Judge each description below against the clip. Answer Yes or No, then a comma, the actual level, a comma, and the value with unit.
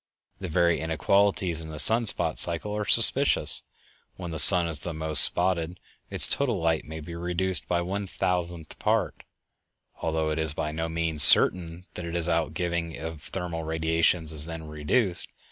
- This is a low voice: Yes, very low, 85 Hz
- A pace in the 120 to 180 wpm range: Yes, average, 160 wpm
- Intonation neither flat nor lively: No, narrow, 2.0 semitones